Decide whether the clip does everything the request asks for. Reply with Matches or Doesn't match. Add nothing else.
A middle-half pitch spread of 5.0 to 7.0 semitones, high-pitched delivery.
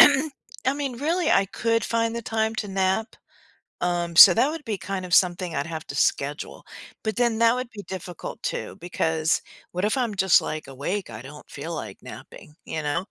Matches